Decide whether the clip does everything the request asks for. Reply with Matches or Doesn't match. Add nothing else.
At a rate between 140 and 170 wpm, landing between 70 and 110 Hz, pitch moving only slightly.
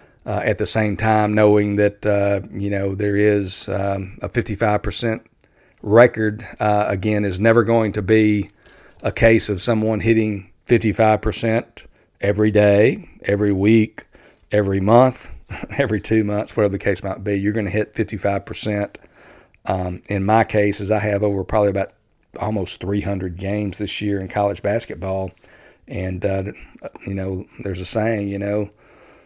Matches